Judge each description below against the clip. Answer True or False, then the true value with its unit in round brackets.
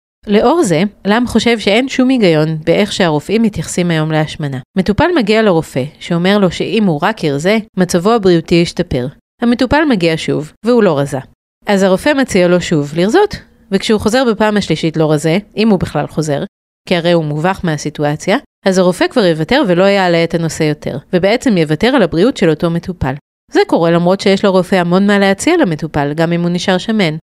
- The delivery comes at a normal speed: False (175 wpm)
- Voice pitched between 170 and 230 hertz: True (185 Hz)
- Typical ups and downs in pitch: True (4.9 semitones)